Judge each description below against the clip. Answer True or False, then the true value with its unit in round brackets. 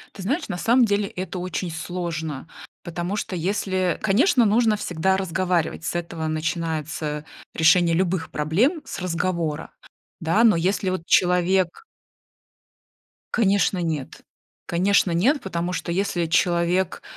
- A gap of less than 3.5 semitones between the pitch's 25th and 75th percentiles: True (2.8 semitones)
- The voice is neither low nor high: True (180 Hz)